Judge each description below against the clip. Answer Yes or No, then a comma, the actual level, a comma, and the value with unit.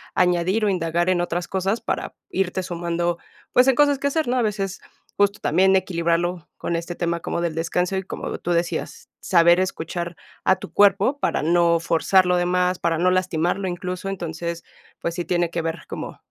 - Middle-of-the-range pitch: Yes, medium, 175 Hz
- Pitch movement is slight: Yes, narrow, 2.0 semitones